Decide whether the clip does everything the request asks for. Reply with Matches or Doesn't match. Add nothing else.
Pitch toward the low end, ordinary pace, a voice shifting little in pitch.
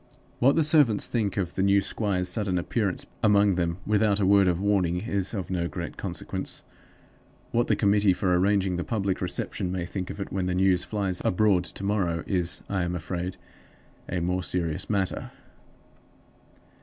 Matches